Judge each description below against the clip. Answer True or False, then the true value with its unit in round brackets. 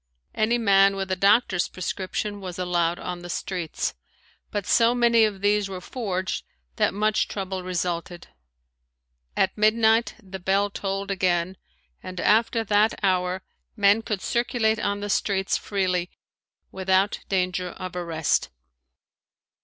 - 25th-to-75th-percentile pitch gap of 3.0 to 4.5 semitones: False (2.5 semitones)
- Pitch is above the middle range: True (195 Hz)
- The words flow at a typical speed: False (130 wpm)